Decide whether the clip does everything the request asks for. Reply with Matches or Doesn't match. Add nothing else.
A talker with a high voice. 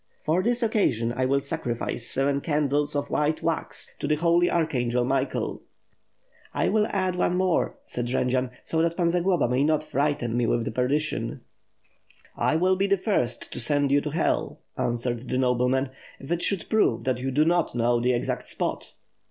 Doesn't match